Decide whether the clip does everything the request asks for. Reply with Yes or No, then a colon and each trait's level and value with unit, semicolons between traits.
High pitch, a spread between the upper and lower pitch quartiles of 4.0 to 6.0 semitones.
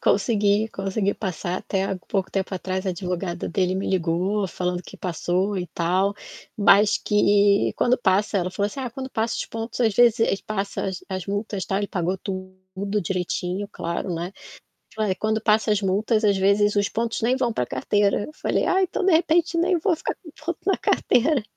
No: high, 200 Hz; average, 2.9 semitones